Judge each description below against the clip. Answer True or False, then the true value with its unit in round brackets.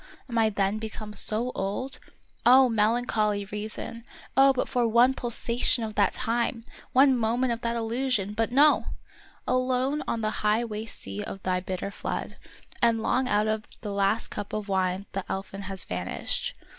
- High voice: True (220 Hz)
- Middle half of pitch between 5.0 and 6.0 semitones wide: False (3.2 semitones)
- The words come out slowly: False (170 wpm)